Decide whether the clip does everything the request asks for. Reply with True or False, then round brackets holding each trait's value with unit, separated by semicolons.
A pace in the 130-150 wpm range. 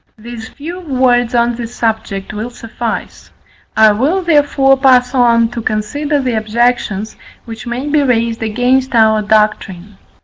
True (140 wpm)